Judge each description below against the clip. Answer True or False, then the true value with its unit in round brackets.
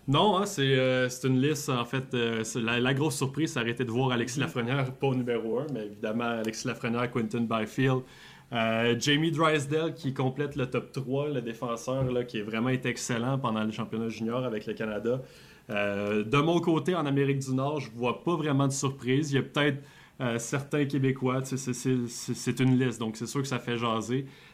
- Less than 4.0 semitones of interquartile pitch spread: True (2.9 semitones)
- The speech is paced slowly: False (220 wpm)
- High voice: False (130 Hz)